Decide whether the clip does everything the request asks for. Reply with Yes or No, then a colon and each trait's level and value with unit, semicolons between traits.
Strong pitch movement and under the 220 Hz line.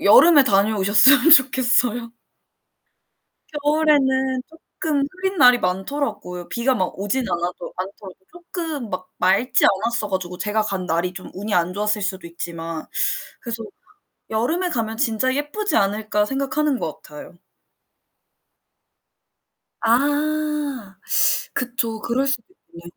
No: wide, 6.3 semitones; high, 230 Hz